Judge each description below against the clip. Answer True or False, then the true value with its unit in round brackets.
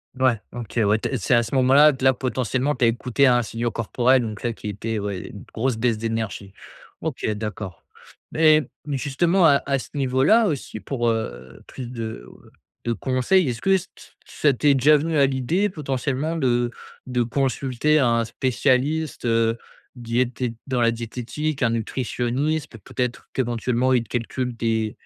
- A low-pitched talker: True (125 Hz)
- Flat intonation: False (3.2 semitones)